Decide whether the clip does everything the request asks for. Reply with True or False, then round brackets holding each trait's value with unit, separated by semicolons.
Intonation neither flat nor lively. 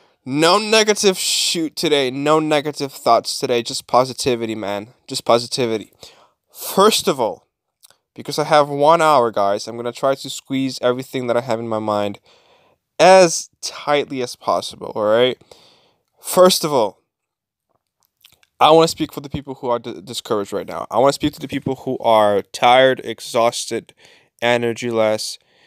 True (4.2 semitones)